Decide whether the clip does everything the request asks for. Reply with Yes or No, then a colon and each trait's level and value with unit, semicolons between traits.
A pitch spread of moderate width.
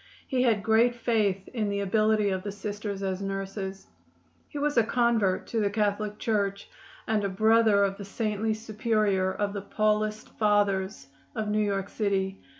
No: narrow, 1.8 semitones